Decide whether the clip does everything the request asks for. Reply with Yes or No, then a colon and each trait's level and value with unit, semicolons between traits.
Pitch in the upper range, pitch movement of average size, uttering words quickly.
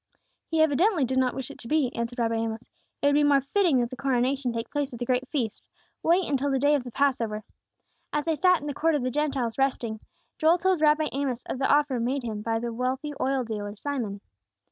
Yes: very high, 265 Hz; average, 3.6 semitones; fast, 230 wpm